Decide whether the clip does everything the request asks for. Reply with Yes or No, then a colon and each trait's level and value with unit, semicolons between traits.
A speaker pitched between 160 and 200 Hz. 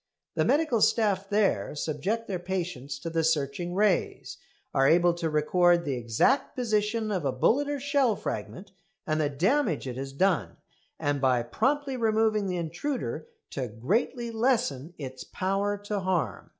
Yes: medium, 185 Hz